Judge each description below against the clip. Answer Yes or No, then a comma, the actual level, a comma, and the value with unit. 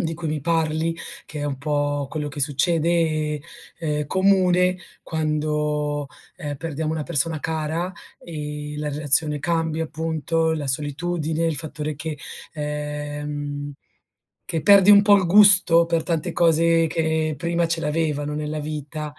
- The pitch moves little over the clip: Yes, narrow, 1.9 semitones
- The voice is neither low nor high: Yes, medium, 155 Hz